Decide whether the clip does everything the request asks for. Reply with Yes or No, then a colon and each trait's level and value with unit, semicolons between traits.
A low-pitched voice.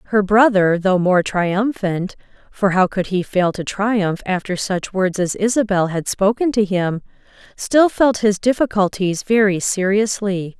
No: high, 200 Hz